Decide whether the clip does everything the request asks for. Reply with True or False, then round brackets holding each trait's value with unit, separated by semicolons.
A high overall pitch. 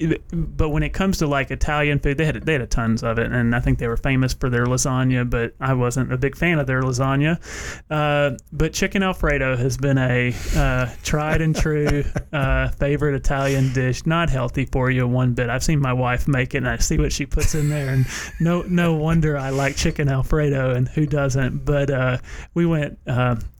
False (140 Hz)